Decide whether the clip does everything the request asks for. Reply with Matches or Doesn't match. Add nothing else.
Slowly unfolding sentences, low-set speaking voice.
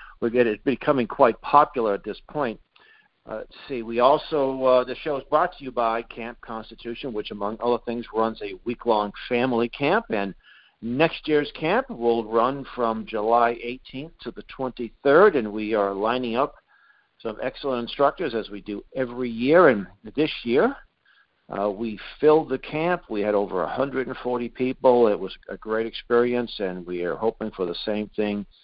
Doesn't match